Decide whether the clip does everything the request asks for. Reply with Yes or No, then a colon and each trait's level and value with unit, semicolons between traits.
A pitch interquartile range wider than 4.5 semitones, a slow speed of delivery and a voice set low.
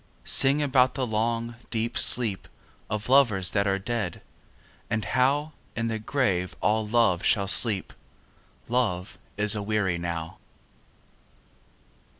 No: average, 3.8 semitones; slow, 120 wpm; low, 110 Hz